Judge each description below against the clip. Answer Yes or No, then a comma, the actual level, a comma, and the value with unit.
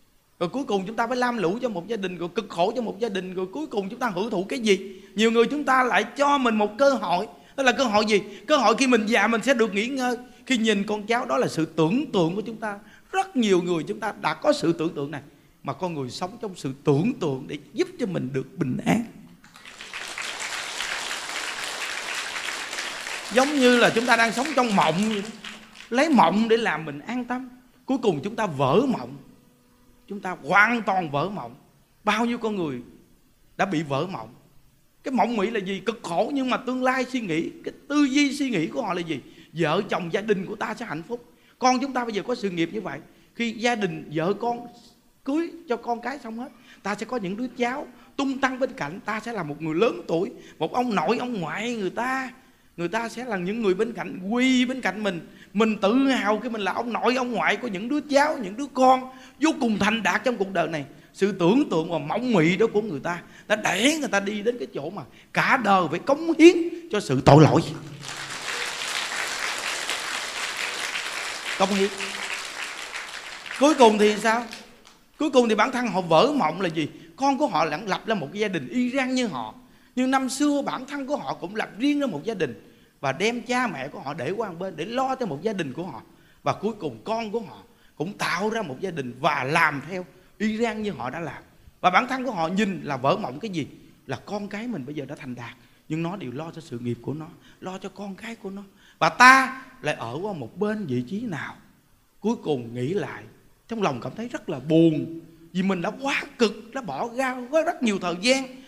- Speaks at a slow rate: No, average, 230 wpm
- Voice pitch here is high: Yes, high, 215 Hz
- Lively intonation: Yes, wide, 6.2 semitones